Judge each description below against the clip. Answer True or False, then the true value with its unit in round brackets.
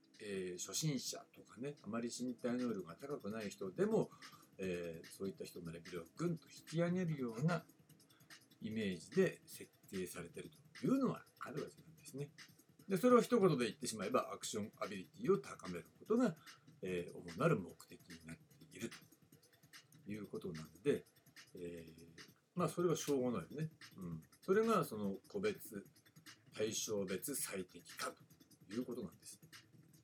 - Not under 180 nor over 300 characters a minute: False (325 characters per minute)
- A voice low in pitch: False (145 Hz)